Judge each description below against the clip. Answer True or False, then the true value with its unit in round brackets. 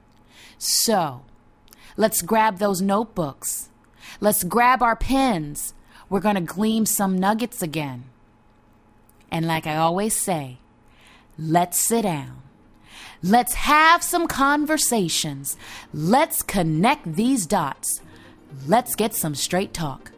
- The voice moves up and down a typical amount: False (8.5 semitones)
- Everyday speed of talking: False (110 wpm)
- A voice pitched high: False (180 Hz)